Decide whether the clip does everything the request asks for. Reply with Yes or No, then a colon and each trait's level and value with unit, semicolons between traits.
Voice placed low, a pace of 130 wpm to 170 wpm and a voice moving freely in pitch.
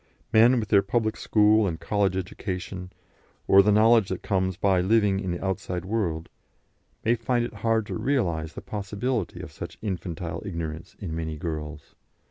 No: very low, 95 Hz; average, 165 wpm; average, 3.8 semitones